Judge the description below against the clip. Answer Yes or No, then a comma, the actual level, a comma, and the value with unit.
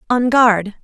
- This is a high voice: Yes, high, 230 Hz